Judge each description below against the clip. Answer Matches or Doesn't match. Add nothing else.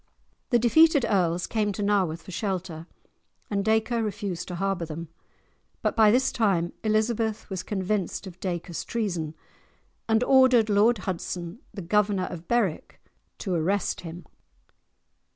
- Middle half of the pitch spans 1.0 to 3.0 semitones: Doesn't match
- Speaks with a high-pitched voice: Matches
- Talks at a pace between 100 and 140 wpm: Matches